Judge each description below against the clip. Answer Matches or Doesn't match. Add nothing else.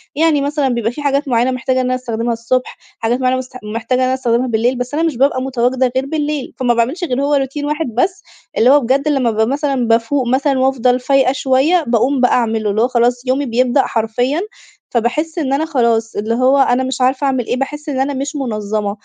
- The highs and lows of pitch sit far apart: Doesn't match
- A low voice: Doesn't match